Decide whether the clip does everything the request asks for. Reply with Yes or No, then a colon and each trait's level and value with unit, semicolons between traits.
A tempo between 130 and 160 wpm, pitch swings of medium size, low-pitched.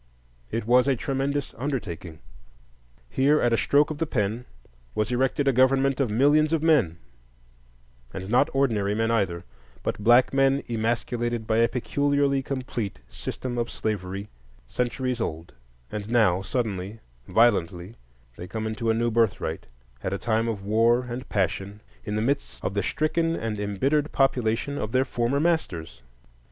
Yes: average, 150 wpm; average, 5.0 semitones; low, 115 Hz